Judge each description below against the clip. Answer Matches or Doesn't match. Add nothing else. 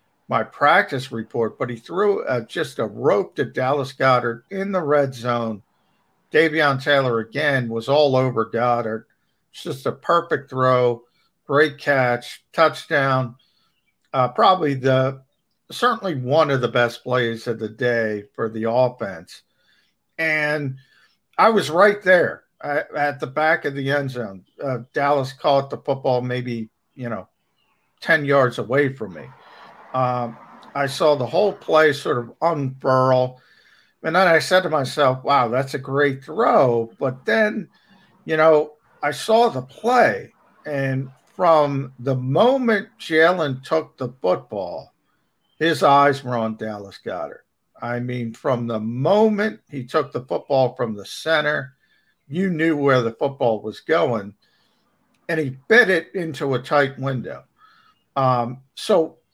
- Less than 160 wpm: Matches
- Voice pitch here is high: Doesn't match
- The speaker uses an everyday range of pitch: Matches